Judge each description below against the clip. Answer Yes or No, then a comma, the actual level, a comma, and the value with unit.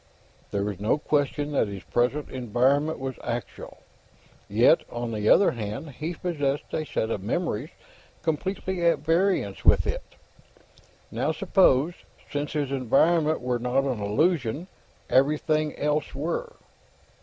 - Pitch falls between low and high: Yes, medium, 145 Hz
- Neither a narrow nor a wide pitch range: Yes, average, 4.7 semitones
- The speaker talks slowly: Yes, slow, 130 wpm